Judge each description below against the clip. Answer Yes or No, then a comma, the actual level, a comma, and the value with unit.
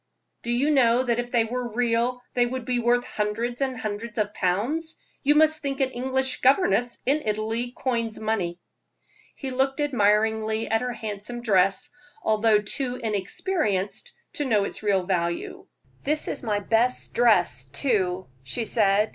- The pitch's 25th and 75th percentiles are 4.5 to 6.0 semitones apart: No, average, 3.5 semitones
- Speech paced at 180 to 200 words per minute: No, average, 155 wpm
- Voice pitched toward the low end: No, high, 235 Hz